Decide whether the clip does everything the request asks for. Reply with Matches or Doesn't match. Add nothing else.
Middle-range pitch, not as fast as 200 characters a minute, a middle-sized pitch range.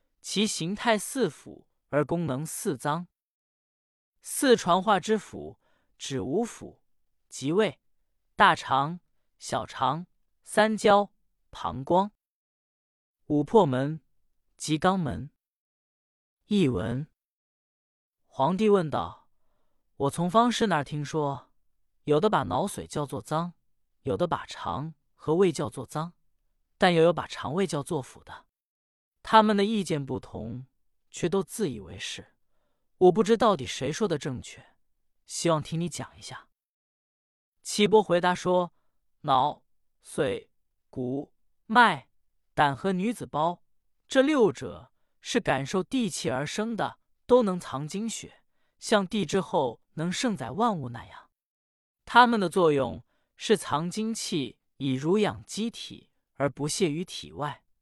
Doesn't match